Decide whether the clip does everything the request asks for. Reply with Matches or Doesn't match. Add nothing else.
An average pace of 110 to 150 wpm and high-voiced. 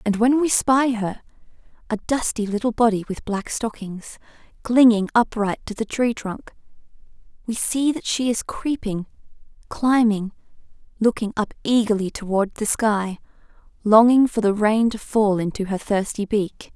Matches